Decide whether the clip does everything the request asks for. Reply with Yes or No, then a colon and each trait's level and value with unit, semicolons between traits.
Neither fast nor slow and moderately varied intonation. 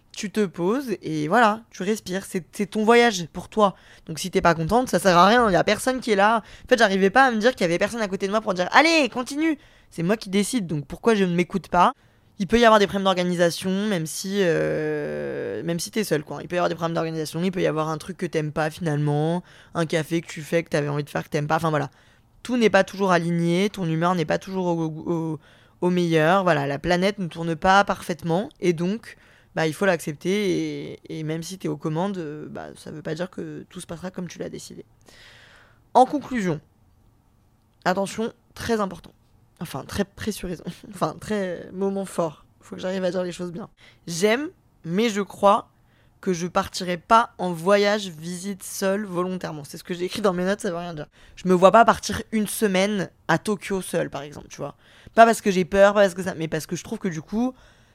No: fast, 235 wpm; average, 3.9 semitones